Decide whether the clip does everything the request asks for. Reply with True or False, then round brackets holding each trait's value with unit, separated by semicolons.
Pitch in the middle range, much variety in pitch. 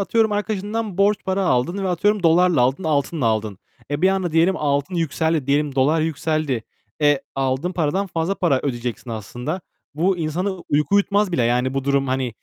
True (160 Hz; 5.7 semitones)